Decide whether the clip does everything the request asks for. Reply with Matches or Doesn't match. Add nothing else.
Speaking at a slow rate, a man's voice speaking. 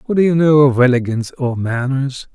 Doesn't match